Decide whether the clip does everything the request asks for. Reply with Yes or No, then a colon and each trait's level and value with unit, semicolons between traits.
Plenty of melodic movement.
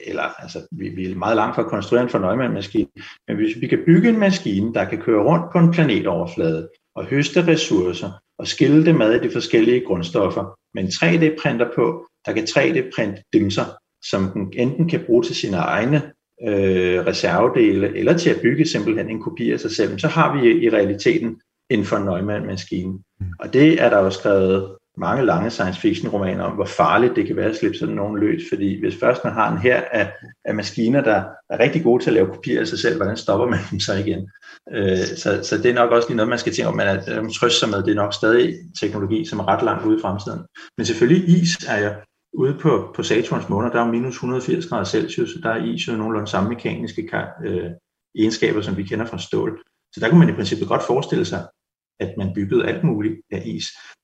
Yes: wide, 8.4 semitones